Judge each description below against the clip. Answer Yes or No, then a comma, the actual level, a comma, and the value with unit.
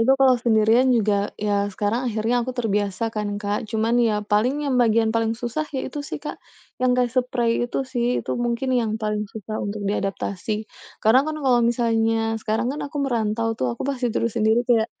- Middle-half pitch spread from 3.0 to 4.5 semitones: No, narrow, 2.6 semitones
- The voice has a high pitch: Yes, high, 225 Hz